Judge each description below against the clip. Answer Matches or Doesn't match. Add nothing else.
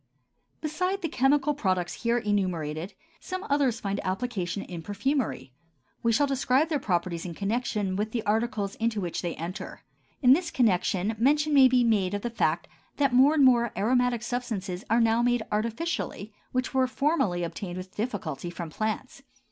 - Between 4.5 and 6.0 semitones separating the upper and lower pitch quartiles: Matches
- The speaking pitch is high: Matches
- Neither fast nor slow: Matches